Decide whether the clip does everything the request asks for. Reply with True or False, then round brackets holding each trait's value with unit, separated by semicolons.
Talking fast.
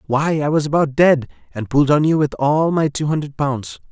True (230 wpm)